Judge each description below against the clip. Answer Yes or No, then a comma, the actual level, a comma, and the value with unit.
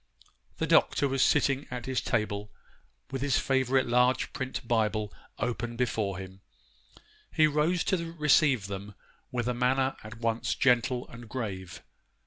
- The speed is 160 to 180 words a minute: No, average, 145 wpm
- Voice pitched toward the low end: Yes, low, 125 Hz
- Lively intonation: No, average, 3.6 semitones